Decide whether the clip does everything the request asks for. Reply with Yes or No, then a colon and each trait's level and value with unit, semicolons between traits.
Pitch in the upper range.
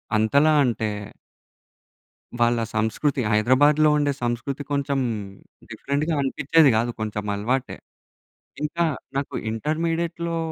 No: medium, 140 Hz